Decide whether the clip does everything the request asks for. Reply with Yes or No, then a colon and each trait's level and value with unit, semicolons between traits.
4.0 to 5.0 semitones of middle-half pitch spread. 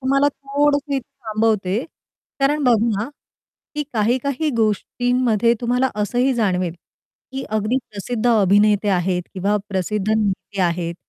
Yes: average, 4.5 semitones